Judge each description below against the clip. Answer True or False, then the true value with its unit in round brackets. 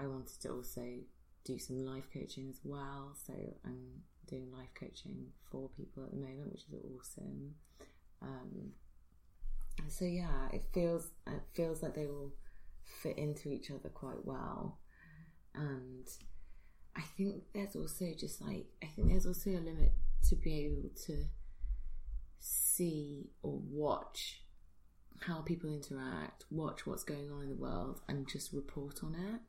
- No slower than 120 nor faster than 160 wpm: True (150 wpm)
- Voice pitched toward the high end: False (140 Hz)